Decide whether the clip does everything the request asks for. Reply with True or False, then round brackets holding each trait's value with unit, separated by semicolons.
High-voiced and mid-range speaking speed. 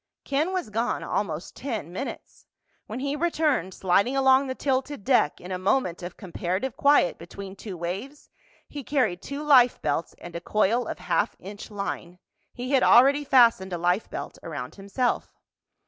True (230 Hz; 165 wpm)